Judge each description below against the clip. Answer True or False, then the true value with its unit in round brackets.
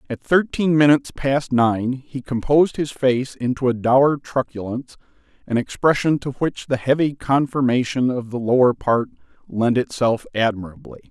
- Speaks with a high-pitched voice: False (130 Hz)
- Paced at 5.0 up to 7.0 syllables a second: False (4.8 syllables/s)